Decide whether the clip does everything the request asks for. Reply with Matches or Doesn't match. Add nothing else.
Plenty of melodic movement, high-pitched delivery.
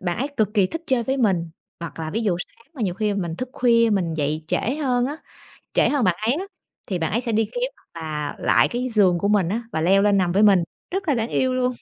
Matches